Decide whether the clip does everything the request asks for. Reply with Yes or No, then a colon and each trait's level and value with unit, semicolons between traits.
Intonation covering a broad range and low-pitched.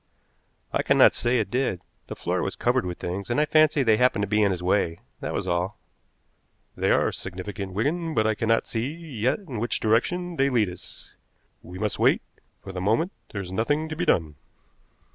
Yes: wide, 6.7 semitones; low, 110 Hz